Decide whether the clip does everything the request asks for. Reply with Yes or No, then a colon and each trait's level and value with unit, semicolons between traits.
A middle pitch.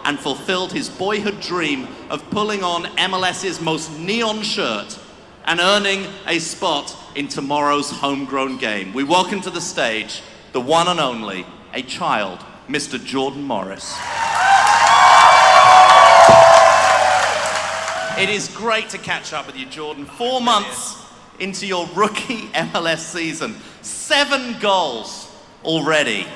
Yes: medium, 180 Hz